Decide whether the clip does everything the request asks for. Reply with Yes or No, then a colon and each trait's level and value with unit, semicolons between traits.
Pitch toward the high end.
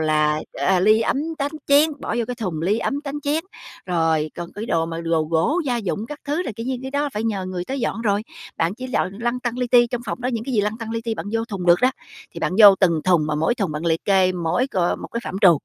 Yes: high, 210 Hz